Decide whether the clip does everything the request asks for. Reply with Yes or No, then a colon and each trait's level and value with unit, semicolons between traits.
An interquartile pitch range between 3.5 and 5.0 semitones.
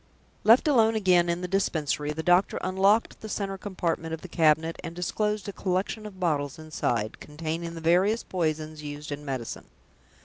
Yes: average, 3.9 semitones